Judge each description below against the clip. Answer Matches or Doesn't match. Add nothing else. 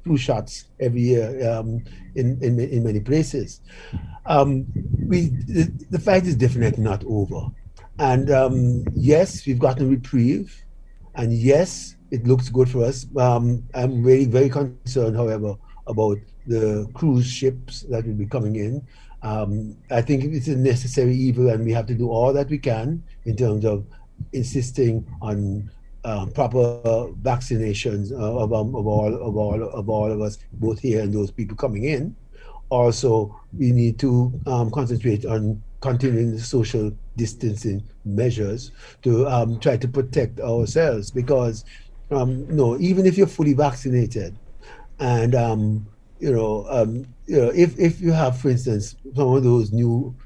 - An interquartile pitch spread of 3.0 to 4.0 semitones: Matches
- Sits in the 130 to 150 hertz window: Doesn't match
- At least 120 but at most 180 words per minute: Matches